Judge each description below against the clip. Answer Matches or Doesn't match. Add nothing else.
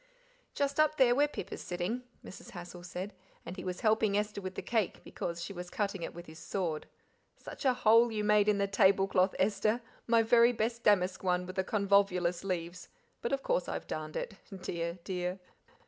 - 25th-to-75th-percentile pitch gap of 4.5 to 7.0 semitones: Doesn't match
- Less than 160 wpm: Doesn't match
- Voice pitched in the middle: Doesn't match